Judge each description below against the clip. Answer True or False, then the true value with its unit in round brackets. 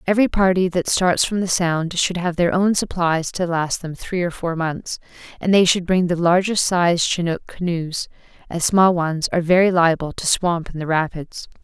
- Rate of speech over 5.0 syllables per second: False (4.7 syllables/s)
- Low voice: False (175 Hz)